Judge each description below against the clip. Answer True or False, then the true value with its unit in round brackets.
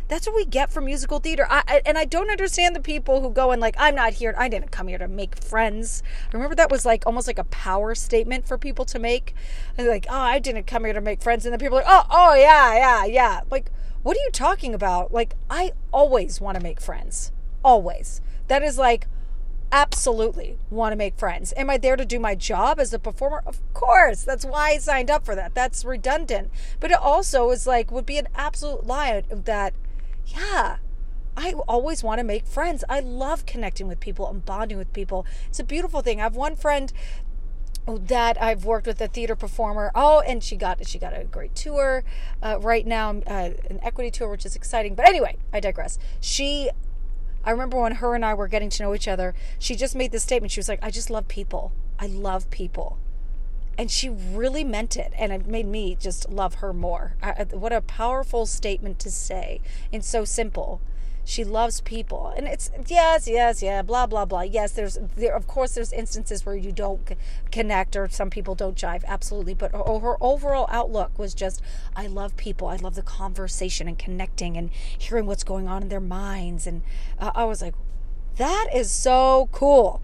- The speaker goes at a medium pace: False (210 wpm)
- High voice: True (230 Hz)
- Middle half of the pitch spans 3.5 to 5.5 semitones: True (5.0 semitones)